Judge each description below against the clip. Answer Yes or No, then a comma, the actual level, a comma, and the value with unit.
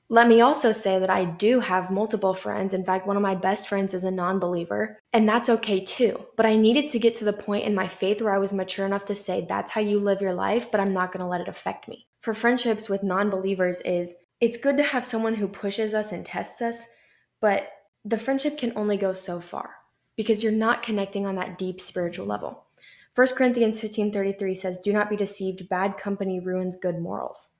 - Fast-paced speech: Yes, fast, 225 wpm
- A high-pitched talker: Yes, high, 200 Hz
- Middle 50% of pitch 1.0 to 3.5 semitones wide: Yes, average, 3.1 semitones